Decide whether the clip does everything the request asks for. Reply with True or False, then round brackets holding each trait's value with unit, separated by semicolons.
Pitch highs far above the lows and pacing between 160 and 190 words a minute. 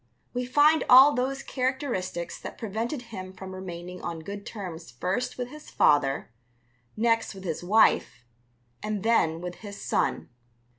False (5.8 semitones; 145 wpm)